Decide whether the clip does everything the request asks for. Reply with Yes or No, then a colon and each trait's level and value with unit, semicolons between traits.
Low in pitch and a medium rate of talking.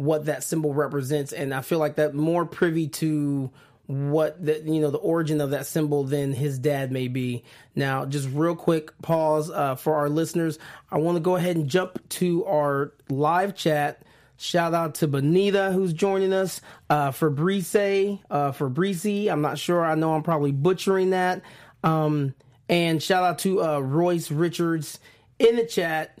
No: medium, 155 Hz; average, 180 wpm